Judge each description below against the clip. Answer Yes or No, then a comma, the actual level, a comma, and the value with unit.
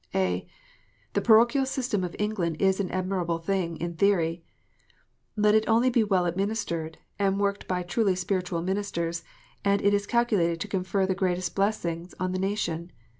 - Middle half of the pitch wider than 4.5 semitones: No, average, 3.0 semitones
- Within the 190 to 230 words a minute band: No, average, 165 wpm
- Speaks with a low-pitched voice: No, high, 190 Hz